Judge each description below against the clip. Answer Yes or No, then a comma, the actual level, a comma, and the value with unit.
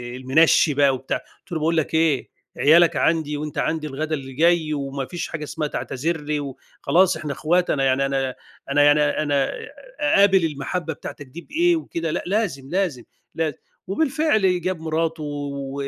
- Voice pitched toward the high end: No, medium, 155 Hz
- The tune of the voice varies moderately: Yes, average, 3.4 semitones